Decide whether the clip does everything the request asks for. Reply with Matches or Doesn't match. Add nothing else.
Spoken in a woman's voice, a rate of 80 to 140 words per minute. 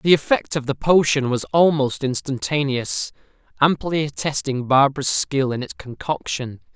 Doesn't match